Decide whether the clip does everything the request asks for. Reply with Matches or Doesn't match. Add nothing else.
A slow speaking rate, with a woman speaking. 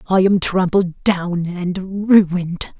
Matches